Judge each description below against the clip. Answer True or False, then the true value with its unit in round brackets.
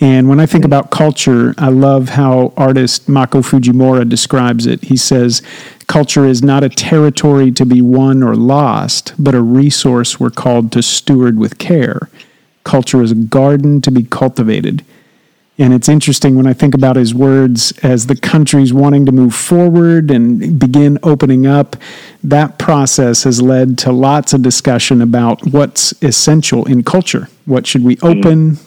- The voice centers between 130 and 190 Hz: True (135 Hz)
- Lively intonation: False (2.4 semitones)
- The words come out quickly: False (165 wpm)